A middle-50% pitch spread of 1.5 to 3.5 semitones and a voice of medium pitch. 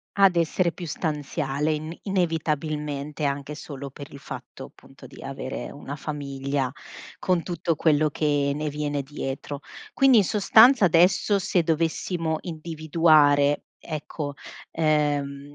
Yes: average, 2.7 semitones; medium, 150 Hz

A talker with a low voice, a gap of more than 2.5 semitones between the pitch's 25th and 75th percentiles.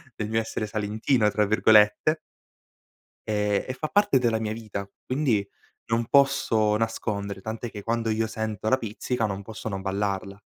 No: low, 110 Hz; narrow, 1.8 semitones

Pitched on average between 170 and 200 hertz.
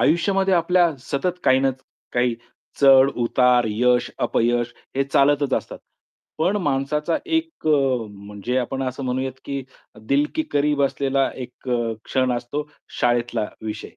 No: low, 135 Hz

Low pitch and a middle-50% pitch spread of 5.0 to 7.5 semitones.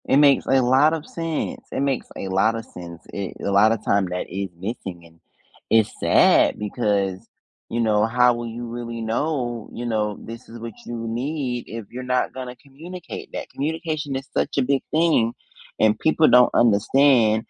No: low, 120 Hz; average, 4.0 semitones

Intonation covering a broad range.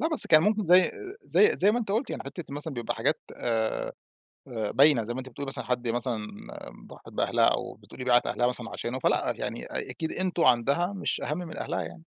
Yes: wide, 6.8 semitones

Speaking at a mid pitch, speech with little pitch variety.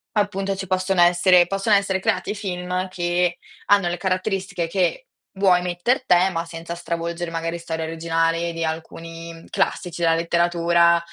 Yes: medium, 175 Hz; narrow, 2.1 semitones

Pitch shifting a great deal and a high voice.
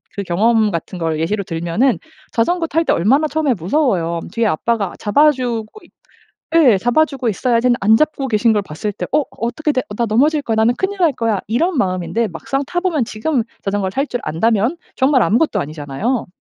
Yes: wide, 6.0 semitones; high, 230 Hz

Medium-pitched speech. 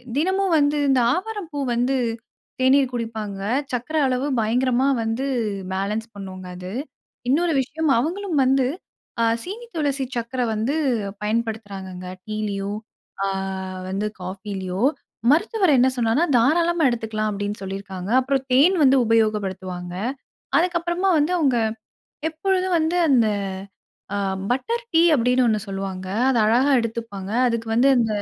No: high, 245 Hz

